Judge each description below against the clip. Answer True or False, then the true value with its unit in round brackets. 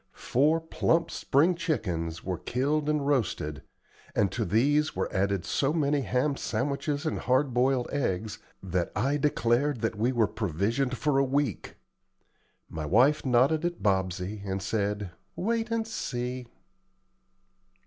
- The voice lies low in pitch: True (125 Hz)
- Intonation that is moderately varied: False (6.2 semitones)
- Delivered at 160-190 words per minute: False (140 wpm)